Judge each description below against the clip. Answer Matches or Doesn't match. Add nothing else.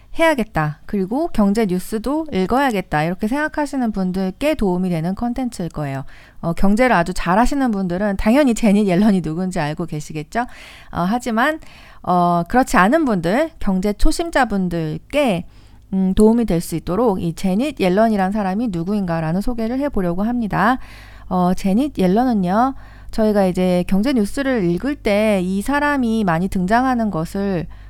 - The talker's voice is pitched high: Matches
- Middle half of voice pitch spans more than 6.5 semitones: Doesn't match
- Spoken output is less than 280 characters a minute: Doesn't match